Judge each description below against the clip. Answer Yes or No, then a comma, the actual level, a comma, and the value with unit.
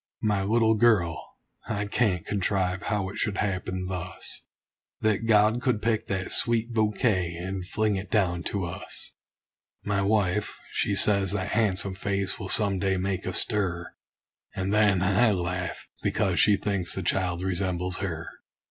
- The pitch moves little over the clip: Yes, narrow, 2.3 semitones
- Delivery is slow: No, average, 155 wpm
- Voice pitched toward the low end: Yes, low, 100 Hz